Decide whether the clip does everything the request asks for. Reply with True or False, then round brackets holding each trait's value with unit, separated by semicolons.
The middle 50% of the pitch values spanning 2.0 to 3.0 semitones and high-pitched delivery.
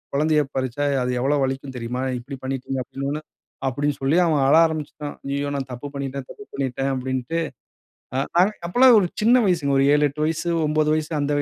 False (2.4 semitones; 140 Hz)